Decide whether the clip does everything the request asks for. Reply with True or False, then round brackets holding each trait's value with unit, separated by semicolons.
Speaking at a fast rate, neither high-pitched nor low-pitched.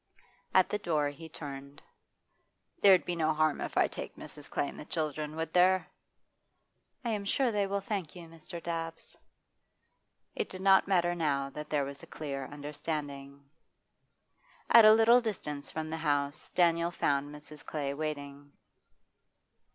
False (160 wpm; 155 Hz)